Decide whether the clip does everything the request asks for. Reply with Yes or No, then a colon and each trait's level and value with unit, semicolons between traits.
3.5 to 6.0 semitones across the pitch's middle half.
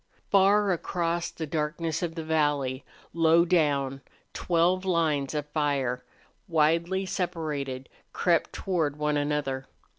No: average, 2.9 semitones